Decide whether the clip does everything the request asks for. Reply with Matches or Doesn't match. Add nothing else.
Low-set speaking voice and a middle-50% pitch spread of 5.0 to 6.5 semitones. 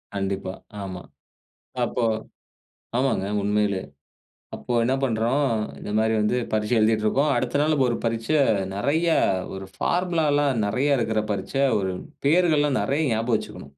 Matches